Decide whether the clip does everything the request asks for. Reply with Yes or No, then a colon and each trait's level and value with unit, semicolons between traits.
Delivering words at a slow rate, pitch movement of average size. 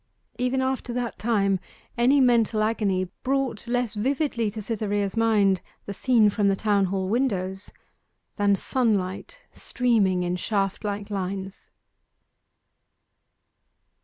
Yes: slow, 115 wpm; average, 3.6 semitones